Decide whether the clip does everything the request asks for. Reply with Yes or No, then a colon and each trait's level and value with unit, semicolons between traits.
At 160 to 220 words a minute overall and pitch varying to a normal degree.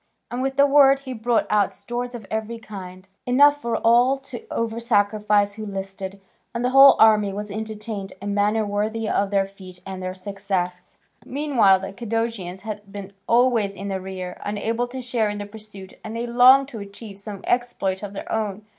Yes: average, 190 wpm; average, 3.2 semitones